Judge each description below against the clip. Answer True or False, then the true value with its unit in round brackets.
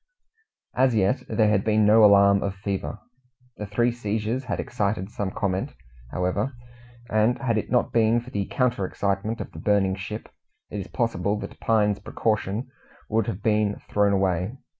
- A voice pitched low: True (105 Hz)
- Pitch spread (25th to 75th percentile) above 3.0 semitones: False (2.4 semitones)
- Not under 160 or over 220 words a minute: True (165 wpm)